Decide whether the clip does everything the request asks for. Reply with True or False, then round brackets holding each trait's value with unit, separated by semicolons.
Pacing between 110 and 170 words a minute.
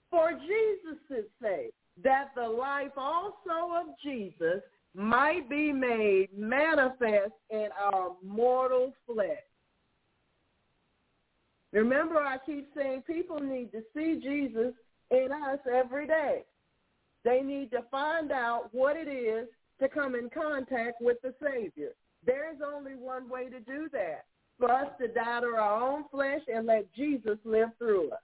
True (140 wpm)